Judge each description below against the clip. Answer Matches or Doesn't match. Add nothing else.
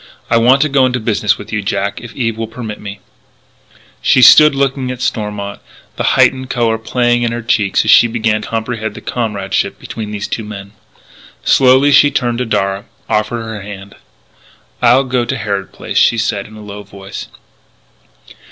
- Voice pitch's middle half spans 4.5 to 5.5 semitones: Doesn't match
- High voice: Doesn't match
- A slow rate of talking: Doesn't match